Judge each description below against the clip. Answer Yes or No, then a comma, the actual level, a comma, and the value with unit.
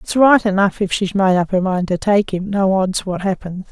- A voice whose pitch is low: No, high, 195 Hz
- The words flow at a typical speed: No, fast, 260 wpm